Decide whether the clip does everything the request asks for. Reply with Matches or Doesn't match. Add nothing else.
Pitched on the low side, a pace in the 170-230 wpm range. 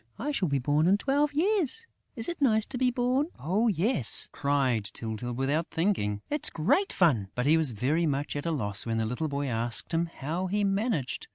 Doesn't match